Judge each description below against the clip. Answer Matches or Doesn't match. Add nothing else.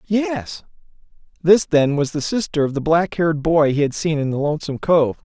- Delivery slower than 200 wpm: Doesn't match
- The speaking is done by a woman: Doesn't match